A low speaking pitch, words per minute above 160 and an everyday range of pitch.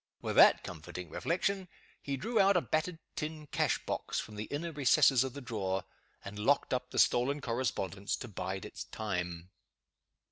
No: low, 125 Hz; average, 170 wpm; wide, 7.5 semitones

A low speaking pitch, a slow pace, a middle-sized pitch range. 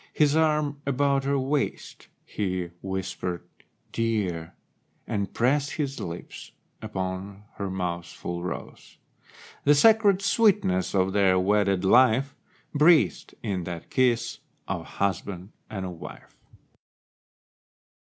No: low, 105 Hz; slow, 110 wpm; wide, 7.2 semitones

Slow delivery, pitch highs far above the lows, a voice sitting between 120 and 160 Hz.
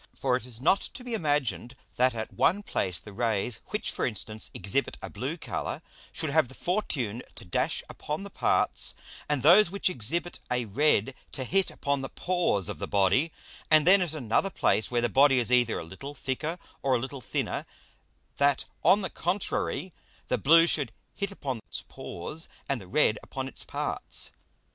No: average, 185 wpm; wide, 5.9 semitones; low, 135 Hz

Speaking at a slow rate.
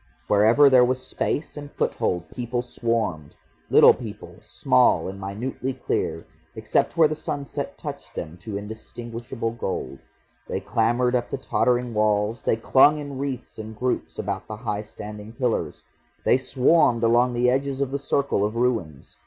No: average, 155 wpm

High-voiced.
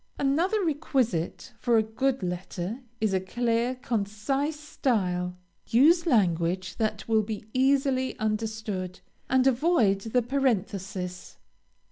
Yes: high, 225 Hz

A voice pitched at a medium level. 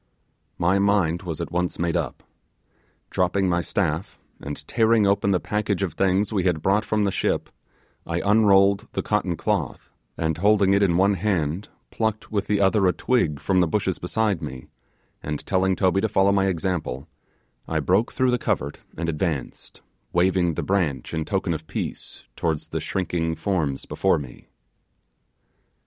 No: very low, 95 Hz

